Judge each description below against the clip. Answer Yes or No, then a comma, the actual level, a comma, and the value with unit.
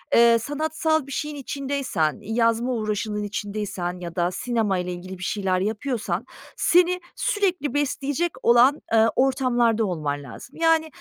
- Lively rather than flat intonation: Yes, wide, 6.4 semitones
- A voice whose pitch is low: No, high, 235 Hz